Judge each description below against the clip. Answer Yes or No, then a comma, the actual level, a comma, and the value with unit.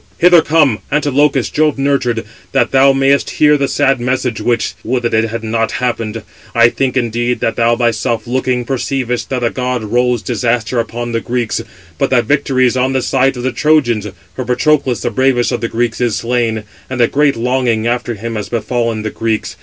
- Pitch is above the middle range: No, low, 120 Hz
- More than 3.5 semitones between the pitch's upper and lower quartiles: No, narrow, 2.4 semitones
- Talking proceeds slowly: No, average, 195 wpm